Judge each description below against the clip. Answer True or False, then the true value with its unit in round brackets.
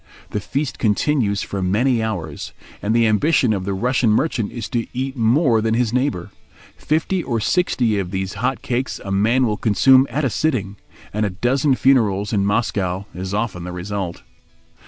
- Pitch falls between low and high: False (110 Hz)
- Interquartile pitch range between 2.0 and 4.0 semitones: False (4.5 semitones)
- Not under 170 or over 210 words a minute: True (180 wpm)